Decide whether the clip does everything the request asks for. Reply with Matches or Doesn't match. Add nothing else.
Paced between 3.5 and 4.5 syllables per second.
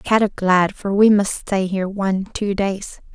Matches